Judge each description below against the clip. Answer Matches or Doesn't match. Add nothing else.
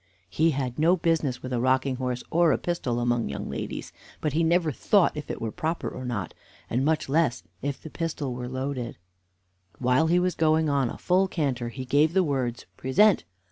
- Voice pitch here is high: Doesn't match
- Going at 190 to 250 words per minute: Matches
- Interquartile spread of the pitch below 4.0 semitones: Doesn't match